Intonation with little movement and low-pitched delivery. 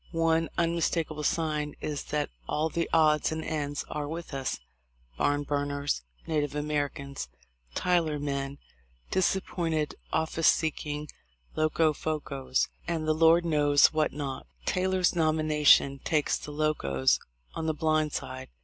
No: narrow, 1.9 semitones; medium, 150 Hz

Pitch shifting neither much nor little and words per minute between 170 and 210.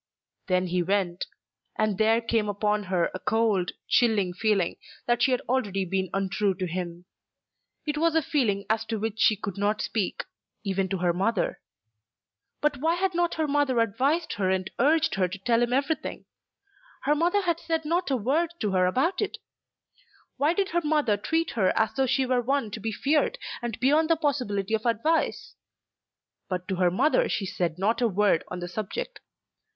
No: wide, 7.1 semitones; average, 190 wpm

